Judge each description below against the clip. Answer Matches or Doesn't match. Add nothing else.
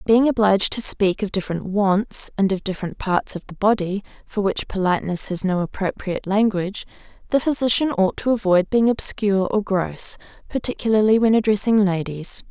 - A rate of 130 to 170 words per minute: Matches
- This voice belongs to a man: Doesn't match